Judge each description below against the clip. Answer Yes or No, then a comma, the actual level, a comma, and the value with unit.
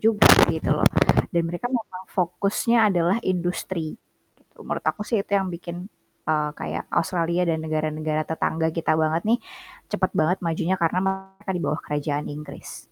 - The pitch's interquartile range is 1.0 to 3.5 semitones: Yes, average, 3.2 semitones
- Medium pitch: Yes, medium, 175 Hz